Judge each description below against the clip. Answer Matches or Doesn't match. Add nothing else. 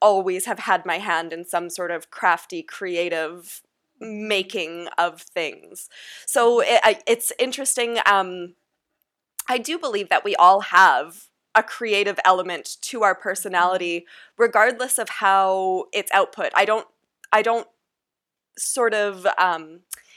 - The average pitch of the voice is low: Doesn't match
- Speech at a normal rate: Doesn't match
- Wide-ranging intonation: Doesn't match